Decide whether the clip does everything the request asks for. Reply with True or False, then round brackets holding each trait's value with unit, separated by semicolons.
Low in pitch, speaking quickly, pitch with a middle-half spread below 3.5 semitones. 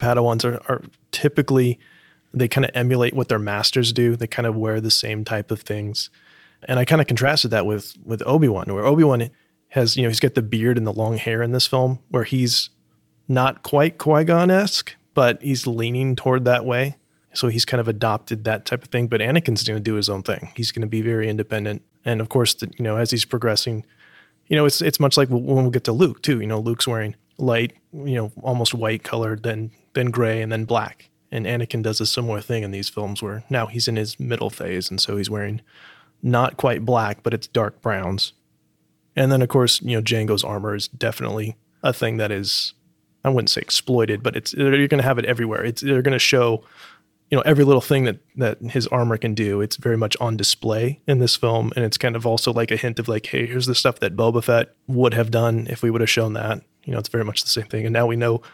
True (115 Hz; 240 wpm; 2.6 semitones)